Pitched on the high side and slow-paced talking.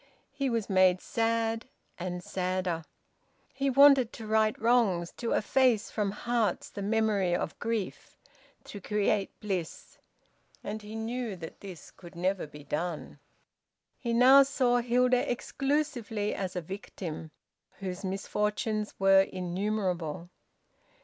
Yes: high, 210 Hz; slow, 125 wpm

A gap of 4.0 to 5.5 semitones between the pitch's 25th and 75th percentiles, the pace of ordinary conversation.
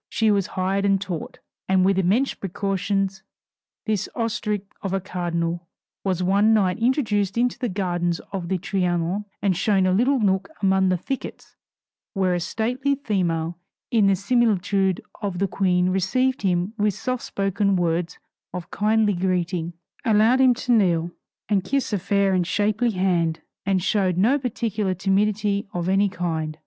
No: average, 2.8 semitones; average, 160 wpm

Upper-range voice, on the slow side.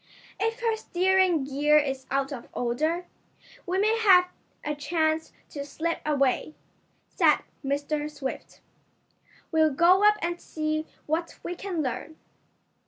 Yes: very high, 315 Hz; slow, 130 wpm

